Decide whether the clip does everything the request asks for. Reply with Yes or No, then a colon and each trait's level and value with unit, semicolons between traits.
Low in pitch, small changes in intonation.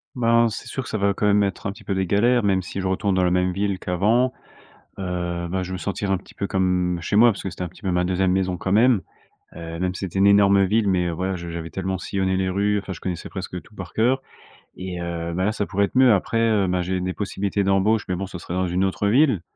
Yes: very low, 95 Hz; narrow, 2.0 semitones